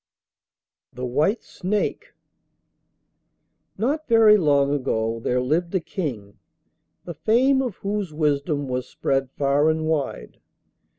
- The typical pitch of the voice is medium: Yes, medium, 150 Hz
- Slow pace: Yes, slow, 115 wpm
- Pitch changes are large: Yes, wide, 6.8 semitones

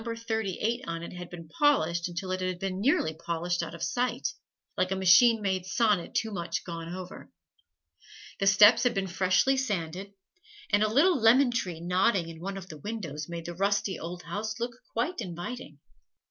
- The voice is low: No, high, 190 Hz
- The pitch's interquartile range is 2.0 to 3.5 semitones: No, average, 4.6 semitones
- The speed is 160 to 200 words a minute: Yes, average, 180 wpm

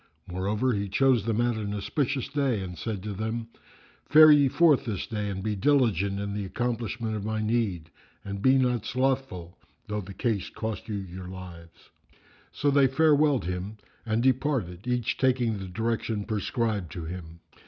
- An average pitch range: Yes, average, 4.5 semitones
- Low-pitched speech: Yes, low, 110 Hz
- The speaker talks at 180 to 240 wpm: No, average, 170 wpm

